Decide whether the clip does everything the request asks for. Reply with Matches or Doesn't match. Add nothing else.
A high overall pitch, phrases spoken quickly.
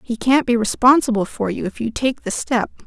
Matches